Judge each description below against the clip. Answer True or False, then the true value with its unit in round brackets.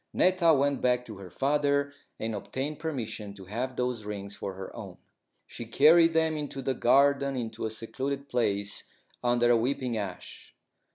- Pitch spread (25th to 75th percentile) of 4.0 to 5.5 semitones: True (4.5 semitones)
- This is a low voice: True (125 Hz)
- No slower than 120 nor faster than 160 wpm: False (170 wpm)